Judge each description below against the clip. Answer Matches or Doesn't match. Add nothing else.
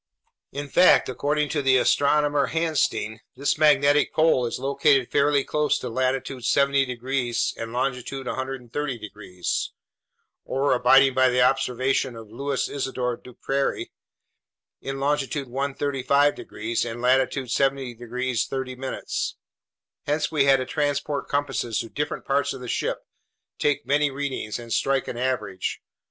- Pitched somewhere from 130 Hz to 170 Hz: Matches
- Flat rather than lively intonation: Matches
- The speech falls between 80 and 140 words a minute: Matches